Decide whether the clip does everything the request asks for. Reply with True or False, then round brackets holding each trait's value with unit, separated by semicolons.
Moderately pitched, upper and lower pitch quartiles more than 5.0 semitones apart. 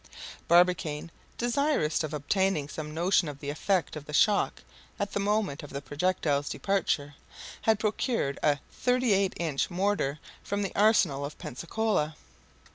True (170 Hz; 5.6 semitones)